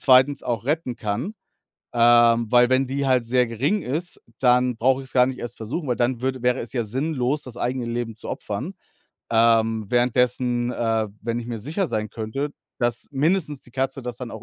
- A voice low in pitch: Yes, low, 125 Hz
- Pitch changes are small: Yes, narrow, 2.2 semitones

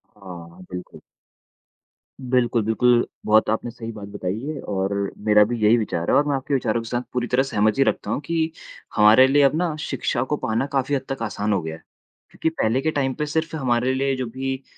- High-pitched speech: No, low, 120 Hz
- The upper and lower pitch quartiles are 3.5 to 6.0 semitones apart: Yes, average, 4.1 semitones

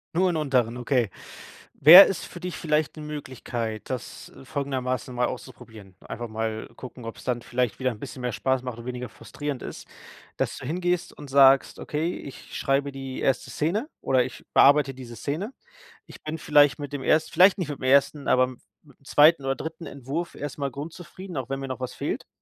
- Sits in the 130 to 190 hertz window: Yes, low, 135 Hz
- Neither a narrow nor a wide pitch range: Yes, average, 3.3 semitones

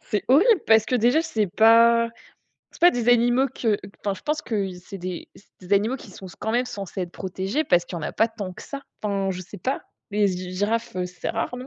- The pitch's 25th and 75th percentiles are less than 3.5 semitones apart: No, average, 4.2 semitones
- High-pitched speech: Yes, high, 210 Hz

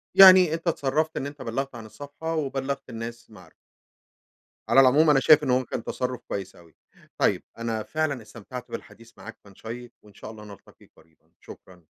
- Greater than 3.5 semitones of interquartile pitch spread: Yes, average, 4.5 semitones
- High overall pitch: No, low, 125 Hz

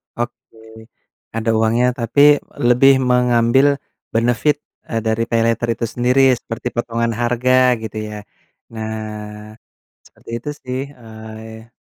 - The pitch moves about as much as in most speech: No, narrow, 1.8 semitones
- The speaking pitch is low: Yes, low, 115 Hz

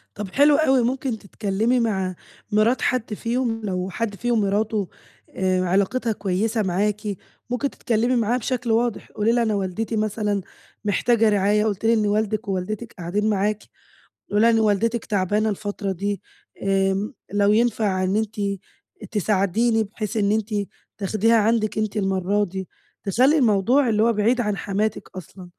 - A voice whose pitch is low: No, high, 215 Hz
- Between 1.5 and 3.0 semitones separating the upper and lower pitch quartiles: Yes, narrow, 2.5 semitones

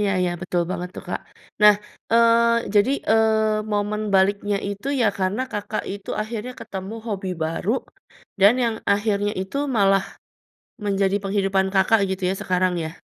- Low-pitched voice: No, high, 205 Hz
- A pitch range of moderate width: No, narrow, 2.2 semitones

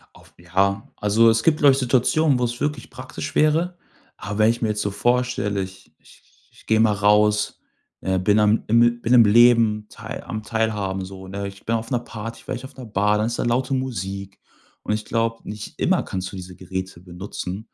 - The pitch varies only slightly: No, average, 3.4 semitones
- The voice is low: Yes, low, 110 Hz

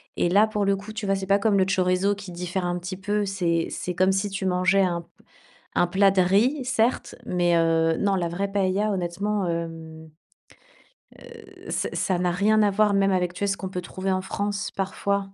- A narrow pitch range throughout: Yes, narrow, 2.2 semitones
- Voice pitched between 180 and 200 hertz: Yes, high, 190 Hz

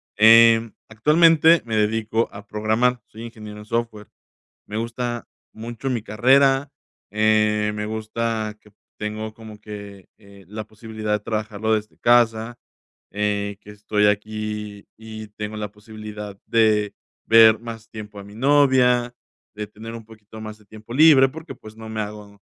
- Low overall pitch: Yes, low, 110 Hz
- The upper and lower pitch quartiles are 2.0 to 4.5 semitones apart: No, narrow, 1.5 semitones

